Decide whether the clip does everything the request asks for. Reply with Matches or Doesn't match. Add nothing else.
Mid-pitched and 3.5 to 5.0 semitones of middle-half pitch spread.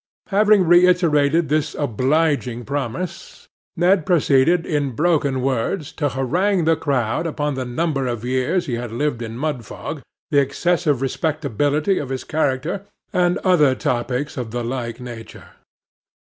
Matches